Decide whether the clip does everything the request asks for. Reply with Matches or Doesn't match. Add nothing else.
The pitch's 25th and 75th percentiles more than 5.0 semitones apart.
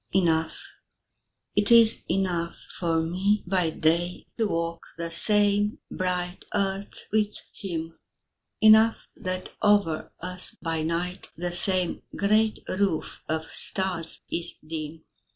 Doesn't match